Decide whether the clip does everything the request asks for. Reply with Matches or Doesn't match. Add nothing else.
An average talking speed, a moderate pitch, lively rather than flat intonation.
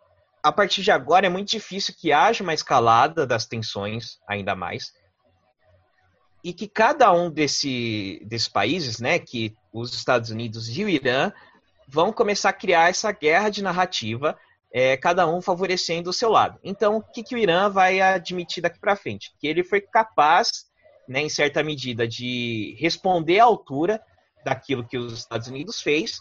Matches